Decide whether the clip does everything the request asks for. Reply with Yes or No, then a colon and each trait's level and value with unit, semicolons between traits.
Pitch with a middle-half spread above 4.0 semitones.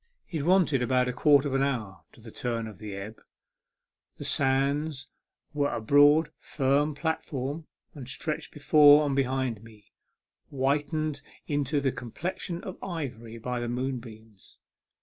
No: average, 3.7 semitones